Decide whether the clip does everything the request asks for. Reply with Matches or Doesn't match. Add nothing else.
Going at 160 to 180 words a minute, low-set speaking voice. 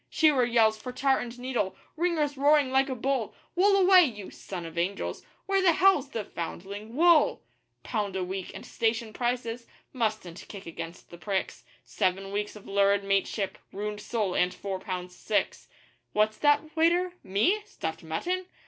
Doesn't match